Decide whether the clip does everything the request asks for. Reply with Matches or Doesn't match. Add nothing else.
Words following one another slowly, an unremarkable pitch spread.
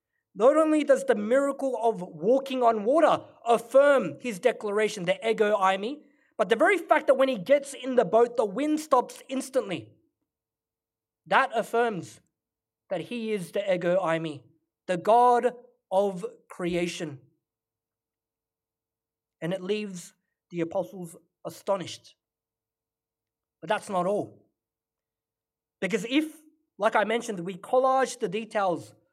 Doesn't match